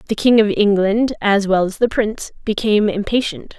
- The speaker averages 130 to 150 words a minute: No, average, 185 wpm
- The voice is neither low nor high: No, high, 210 Hz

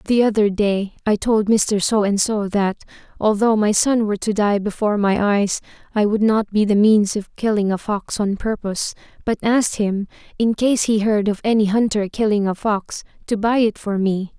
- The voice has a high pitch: Yes, high, 210 Hz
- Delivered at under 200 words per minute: No, fast, 205 wpm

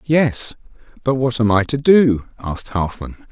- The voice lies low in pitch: Yes, low, 125 Hz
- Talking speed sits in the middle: Yes, average, 165 wpm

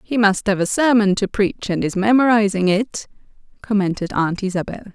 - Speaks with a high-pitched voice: Yes, high, 205 Hz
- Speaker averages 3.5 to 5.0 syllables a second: No, 5.5 syllables/s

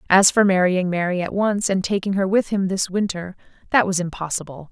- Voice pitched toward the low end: No, medium, 185 Hz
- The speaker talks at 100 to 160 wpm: No, fast, 205 wpm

